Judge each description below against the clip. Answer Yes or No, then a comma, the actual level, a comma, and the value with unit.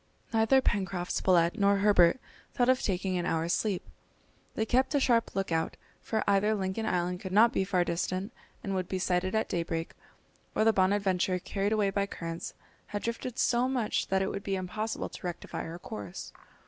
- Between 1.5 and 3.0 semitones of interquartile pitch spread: No, average, 3.4 semitones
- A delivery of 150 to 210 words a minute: Yes, average, 185 wpm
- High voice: Yes, high, 195 Hz